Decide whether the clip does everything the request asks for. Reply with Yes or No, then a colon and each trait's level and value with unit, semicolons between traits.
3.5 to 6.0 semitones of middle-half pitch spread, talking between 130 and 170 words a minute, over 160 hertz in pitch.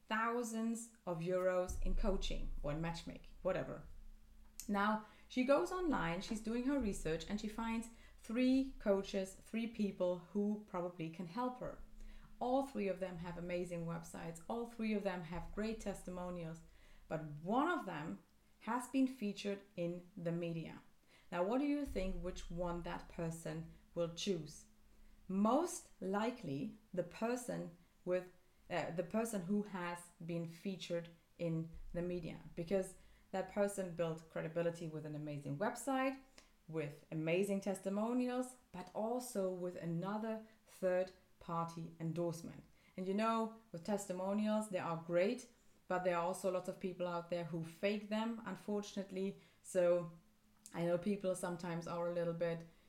Yes: average, 3.9 semitones; average, 145 wpm; medium, 185 Hz